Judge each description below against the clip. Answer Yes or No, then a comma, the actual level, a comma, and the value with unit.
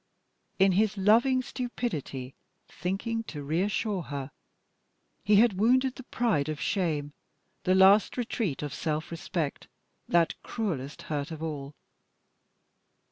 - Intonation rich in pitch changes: Yes, wide, 6.7 semitones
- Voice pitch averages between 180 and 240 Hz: Yes, medium, 185 Hz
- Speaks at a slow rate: Yes, slow, 120 wpm